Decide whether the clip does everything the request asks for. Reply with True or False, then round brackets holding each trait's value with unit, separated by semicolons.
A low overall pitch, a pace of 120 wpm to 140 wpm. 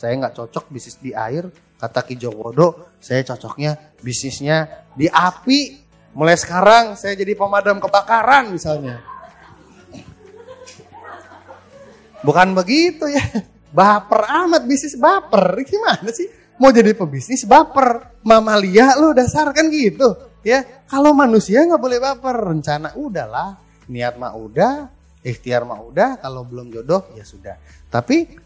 False (200 Hz; 125 wpm)